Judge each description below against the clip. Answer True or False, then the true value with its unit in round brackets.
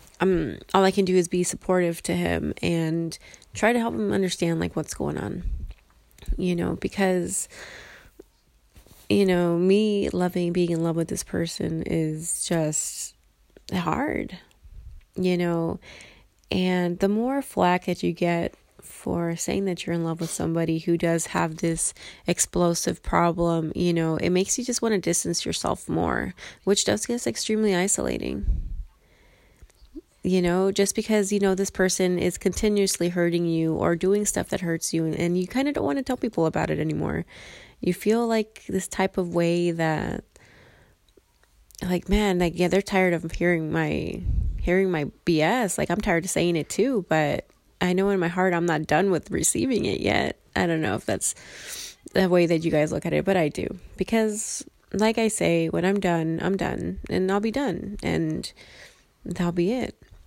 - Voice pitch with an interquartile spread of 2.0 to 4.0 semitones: True (2.7 semitones)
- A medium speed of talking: True (180 wpm)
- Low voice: False (180 Hz)